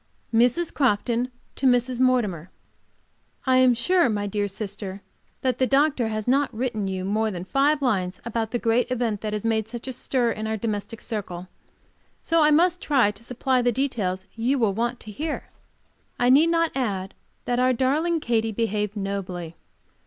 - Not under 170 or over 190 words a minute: Yes, average, 175 wpm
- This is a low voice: No, high, 235 Hz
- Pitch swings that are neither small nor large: Yes, average, 3.8 semitones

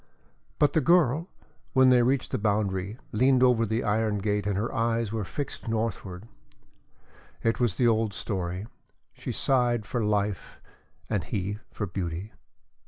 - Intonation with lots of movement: No, average, 3.2 semitones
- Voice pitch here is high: No, low, 110 Hz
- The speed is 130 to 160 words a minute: Yes, average, 150 wpm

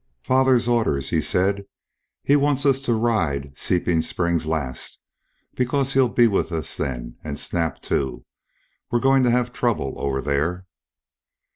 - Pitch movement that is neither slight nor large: No, wide, 8.8 semitones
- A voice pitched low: Yes, very low, 95 Hz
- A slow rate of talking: No, average, 145 wpm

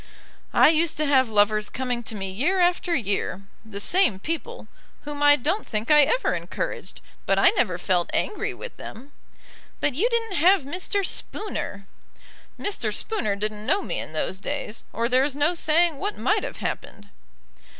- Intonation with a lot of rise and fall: Yes, wide, 8.8 semitones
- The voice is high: Yes, very high, 285 Hz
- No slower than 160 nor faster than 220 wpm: Yes, average, 170 wpm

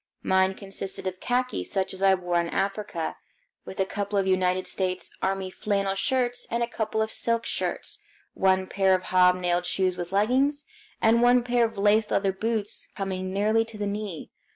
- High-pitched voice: Yes, high, 195 Hz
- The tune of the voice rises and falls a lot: No, average, 2.9 semitones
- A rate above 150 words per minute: Yes, average, 185 wpm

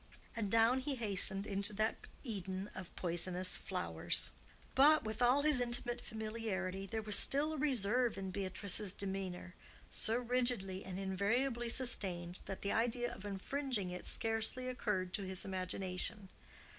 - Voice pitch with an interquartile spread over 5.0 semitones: No, average, 4.2 semitones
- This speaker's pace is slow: No, average, 145 wpm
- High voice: Yes, high, 210 Hz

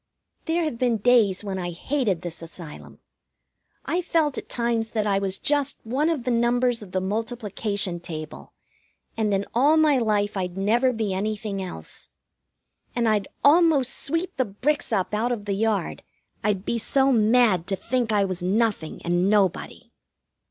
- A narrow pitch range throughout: No, average, 4.4 semitones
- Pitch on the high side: Yes, high, 215 Hz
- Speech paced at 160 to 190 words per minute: Yes, average, 165 wpm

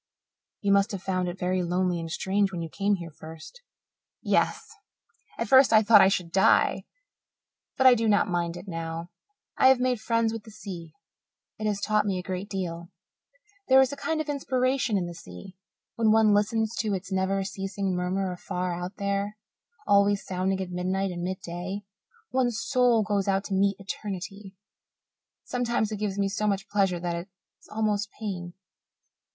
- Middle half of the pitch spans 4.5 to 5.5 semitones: No, average, 3.0 semitones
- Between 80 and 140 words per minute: No, average, 180 wpm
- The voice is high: Yes, high, 195 Hz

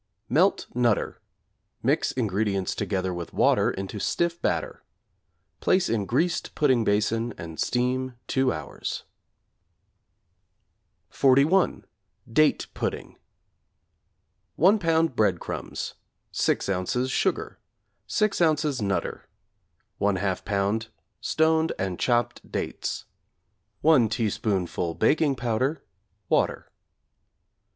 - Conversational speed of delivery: No, slow, 90 wpm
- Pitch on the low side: Yes, low, 120 Hz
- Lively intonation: Yes, wide, 7.1 semitones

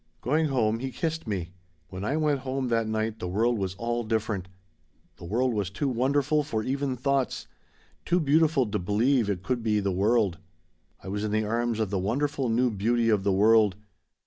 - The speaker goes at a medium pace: Yes, average, 195 wpm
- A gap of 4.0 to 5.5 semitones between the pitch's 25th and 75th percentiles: Yes, average, 4.3 semitones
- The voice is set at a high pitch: No, low, 115 Hz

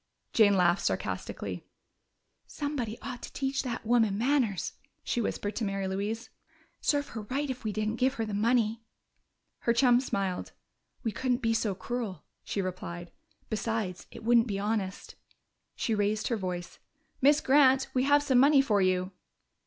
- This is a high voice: Yes, high, 225 Hz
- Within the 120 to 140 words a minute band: No, average, 160 wpm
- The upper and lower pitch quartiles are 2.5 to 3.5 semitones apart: No, average, 4.0 semitones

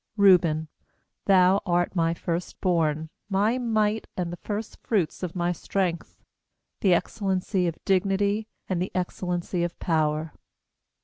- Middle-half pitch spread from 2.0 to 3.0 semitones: Yes, average, 2.7 semitones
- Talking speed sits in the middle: No, slow, 130 wpm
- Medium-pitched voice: Yes, medium, 180 Hz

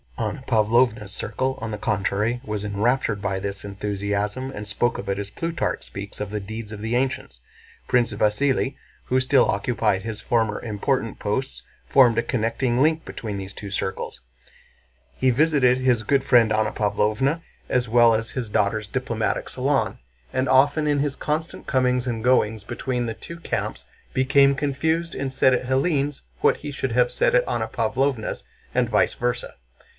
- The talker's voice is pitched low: Yes, low, 120 Hz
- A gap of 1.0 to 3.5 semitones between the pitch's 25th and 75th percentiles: No, average, 4.0 semitones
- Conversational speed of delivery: Yes, average, 170 wpm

